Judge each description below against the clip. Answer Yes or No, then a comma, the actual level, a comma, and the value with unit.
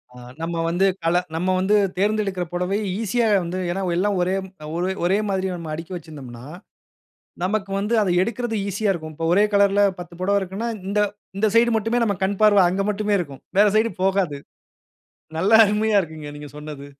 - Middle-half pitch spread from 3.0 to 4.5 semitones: Yes, average, 3.3 semitones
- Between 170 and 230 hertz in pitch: Yes, high, 190 Hz